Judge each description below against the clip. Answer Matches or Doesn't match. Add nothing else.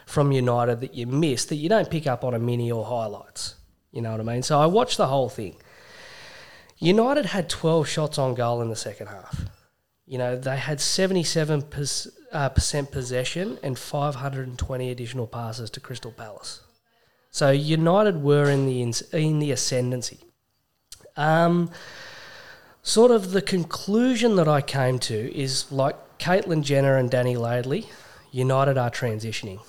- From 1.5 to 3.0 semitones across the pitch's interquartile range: Doesn't match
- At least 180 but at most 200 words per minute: Doesn't match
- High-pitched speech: Doesn't match